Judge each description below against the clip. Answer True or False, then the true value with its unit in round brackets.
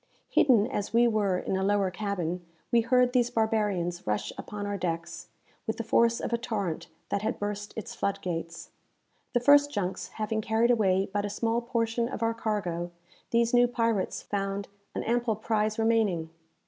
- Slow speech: False (175 wpm)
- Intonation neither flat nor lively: True (3.2 semitones)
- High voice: True (215 Hz)